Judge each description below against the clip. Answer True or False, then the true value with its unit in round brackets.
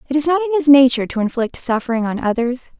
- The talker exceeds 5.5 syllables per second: True (7.3 syllables/s)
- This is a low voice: False (265 Hz)